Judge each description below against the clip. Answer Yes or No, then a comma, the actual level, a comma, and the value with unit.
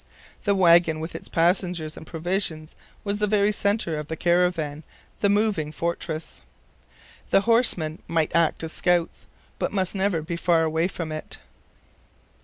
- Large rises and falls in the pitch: No, average, 3.5 semitones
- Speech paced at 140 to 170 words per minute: Yes, average, 150 wpm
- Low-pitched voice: No, medium, 170 Hz